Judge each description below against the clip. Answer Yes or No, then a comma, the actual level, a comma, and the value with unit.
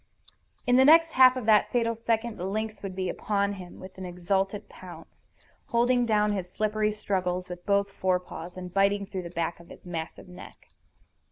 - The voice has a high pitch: Yes, high, 200 Hz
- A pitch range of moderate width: Yes, average, 3.2 semitones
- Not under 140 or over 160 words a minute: No, average, 185 wpm